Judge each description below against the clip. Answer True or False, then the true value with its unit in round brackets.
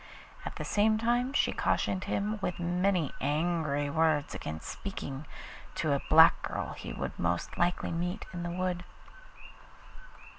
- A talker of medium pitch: True (175 Hz)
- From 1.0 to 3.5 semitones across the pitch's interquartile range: False (4.3 semitones)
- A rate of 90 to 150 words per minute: True (145 wpm)